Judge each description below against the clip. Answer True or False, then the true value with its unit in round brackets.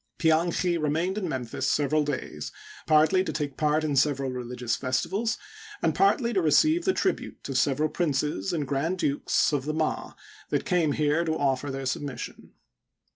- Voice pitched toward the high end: False (150 Hz)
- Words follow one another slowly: False (165 wpm)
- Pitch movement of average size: True (3.8 semitones)